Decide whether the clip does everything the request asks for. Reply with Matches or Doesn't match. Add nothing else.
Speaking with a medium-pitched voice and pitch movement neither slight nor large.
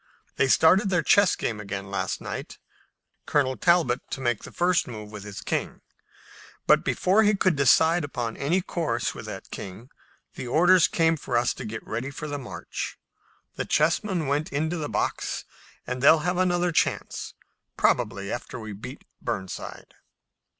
Doesn't match